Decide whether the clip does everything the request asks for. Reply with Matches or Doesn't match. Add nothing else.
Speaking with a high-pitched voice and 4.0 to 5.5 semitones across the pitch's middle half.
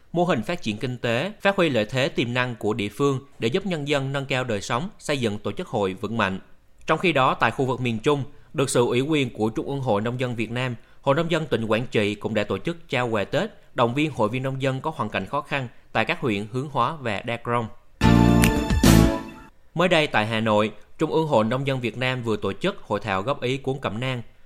Doesn't match